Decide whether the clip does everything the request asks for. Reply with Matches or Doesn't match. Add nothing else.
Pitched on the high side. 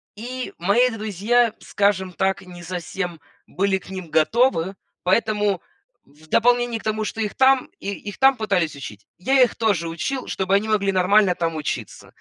Matches